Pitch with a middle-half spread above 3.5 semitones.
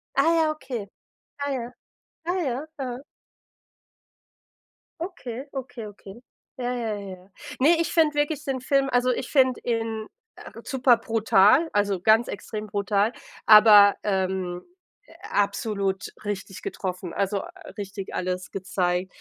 Yes: average, 4.9 semitones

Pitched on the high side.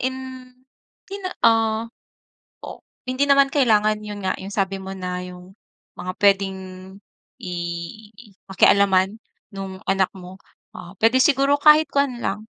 Yes: high, 200 Hz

